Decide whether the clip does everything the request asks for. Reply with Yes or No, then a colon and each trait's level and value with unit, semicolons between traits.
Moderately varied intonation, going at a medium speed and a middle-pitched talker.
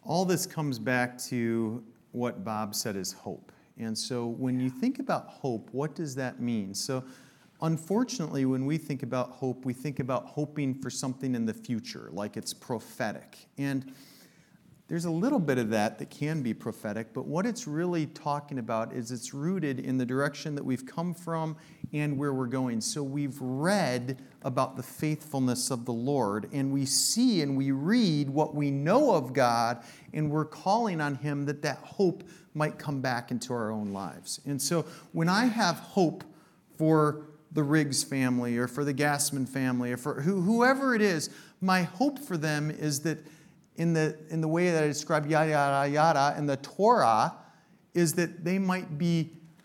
Yes: average, 4.1 semitones; average, 180 wpm; medium, 145 Hz